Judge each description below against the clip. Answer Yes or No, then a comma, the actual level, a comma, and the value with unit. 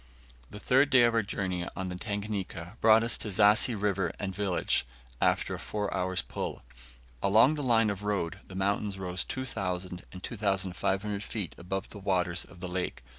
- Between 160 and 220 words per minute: Yes, average, 175 wpm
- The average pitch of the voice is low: Yes, low, 100 Hz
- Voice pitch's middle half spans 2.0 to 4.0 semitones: Yes, narrow, 2.6 semitones